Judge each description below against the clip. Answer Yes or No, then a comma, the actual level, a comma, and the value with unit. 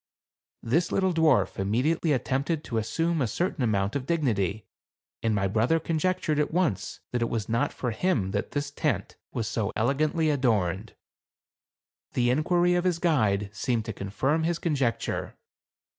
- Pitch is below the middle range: Yes, low, 130 Hz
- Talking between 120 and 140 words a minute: No, average, 160 wpm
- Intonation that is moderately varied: No, wide, 6.8 semitones